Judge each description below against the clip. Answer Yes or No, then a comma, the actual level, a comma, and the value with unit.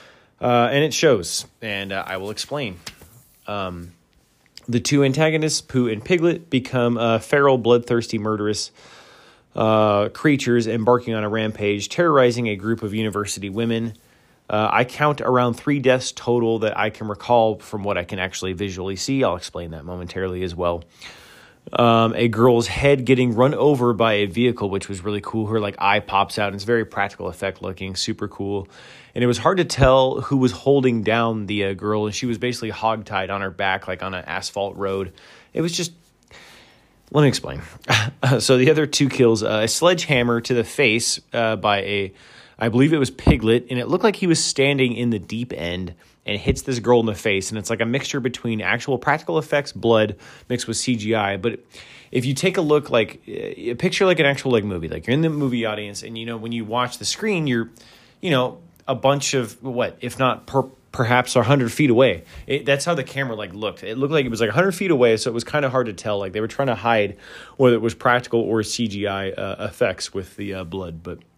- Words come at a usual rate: No, fast, 210 wpm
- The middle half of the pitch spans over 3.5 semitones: Yes, average, 4.1 semitones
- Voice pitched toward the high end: No, low, 115 Hz